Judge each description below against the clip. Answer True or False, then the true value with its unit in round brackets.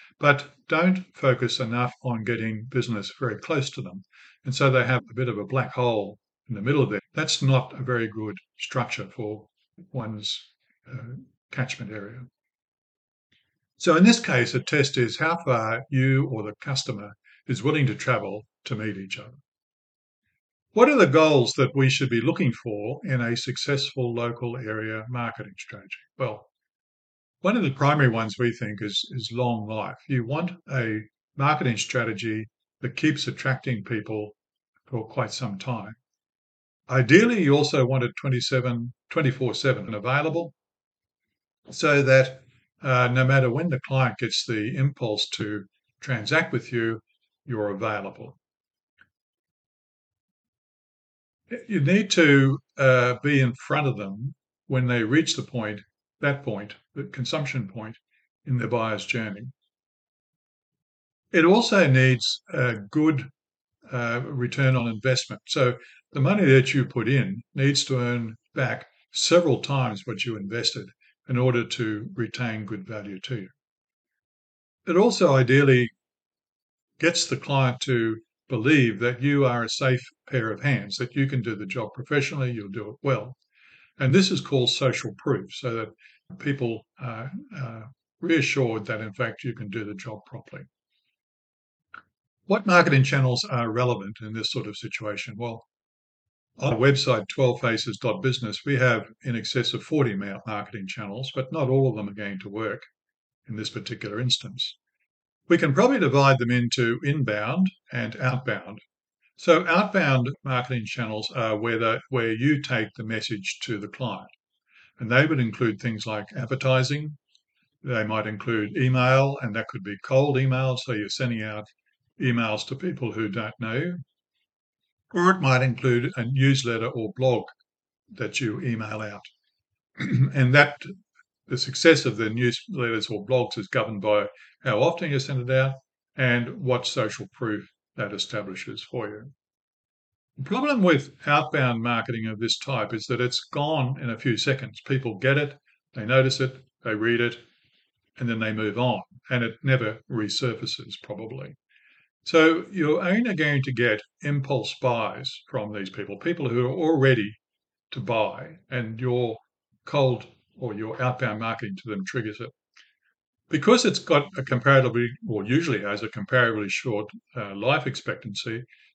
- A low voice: True (125 Hz)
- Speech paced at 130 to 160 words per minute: True (155 wpm)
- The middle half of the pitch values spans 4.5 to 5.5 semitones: False (3.5 semitones)